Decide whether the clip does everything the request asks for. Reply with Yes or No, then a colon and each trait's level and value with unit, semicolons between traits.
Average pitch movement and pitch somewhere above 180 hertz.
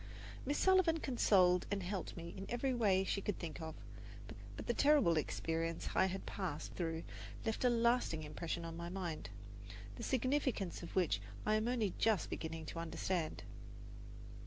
No: wide, 6.0 semitones; high, 190 Hz